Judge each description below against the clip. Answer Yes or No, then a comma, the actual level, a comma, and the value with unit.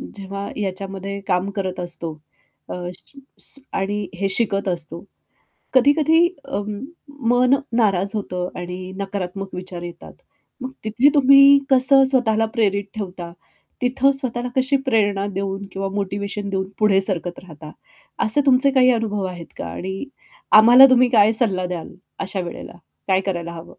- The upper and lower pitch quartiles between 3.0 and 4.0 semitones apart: No, average, 4.6 semitones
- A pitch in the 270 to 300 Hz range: No, high, 200 Hz